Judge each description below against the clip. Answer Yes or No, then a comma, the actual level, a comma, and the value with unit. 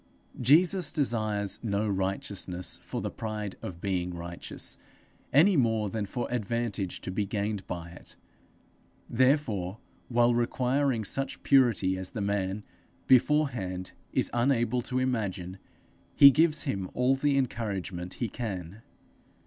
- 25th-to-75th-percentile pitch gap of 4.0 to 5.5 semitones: Yes, average, 5.1 semitones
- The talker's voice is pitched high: No, low, 110 Hz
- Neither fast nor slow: No, slow, 125 wpm